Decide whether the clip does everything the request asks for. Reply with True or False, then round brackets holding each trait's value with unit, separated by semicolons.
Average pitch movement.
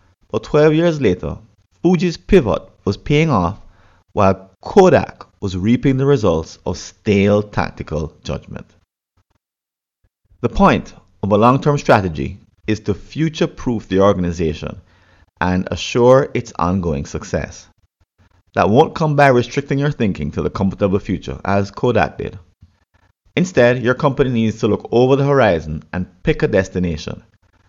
False (5.7 semitones)